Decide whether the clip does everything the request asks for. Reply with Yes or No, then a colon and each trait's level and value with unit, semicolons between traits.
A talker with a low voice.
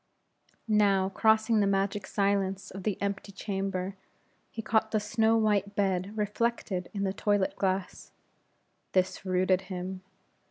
No: high, 200 Hz